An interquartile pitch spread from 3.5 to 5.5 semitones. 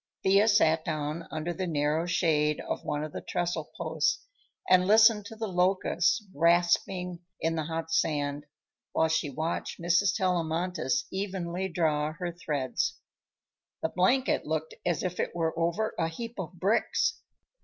No: average, 2.8 semitones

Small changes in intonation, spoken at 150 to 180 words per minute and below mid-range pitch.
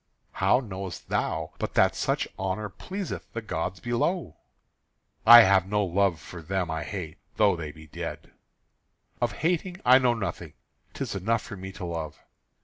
No: average, 4.8 semitones; average, 160 wpm; low, 100 Hz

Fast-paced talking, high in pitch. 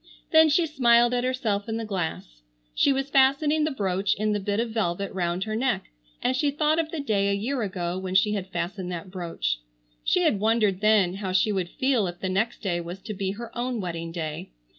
Yes: fast, 225 wpm; high, 205 Hz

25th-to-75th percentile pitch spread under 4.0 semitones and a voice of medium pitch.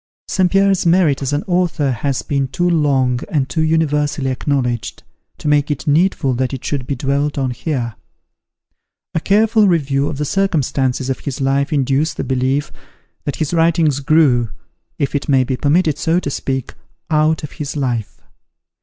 Yes: average, 3.2 semitones; medium, 145 Hz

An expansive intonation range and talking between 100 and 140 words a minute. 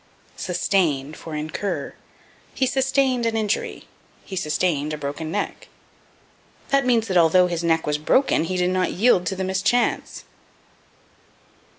Yes: wide, 5.8 semitones; slow, 135 wpm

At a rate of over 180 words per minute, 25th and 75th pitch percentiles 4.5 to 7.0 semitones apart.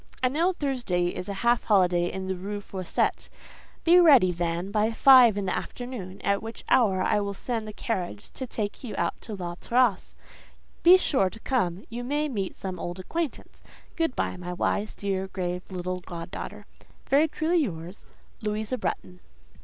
No: average, 175 wpm; wide, 5.5 semitones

